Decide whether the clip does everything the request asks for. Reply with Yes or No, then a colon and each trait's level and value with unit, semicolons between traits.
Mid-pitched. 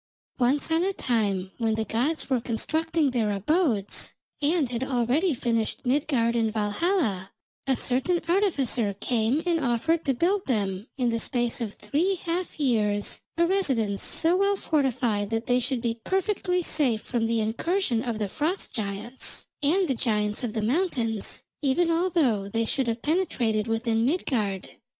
No: high, 245 Hz